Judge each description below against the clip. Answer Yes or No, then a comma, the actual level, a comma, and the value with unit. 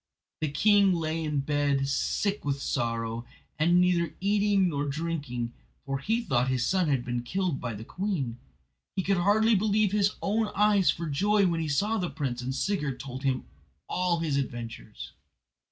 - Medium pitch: Yes, medium, 160 Hz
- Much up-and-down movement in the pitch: Yes, wide, 6.6 semitones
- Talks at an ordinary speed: Yes, average, 175 wpm